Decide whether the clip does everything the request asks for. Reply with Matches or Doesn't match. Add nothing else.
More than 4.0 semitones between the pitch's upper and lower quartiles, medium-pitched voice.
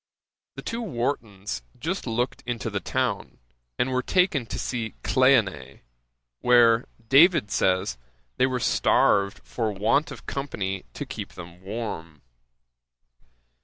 Doesn't match